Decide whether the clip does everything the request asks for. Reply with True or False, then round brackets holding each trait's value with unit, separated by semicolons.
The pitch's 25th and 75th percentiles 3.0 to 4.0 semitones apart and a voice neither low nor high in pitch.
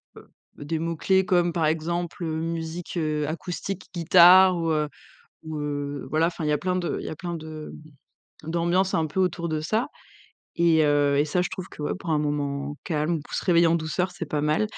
False (2.4 semitones; 165 Hz)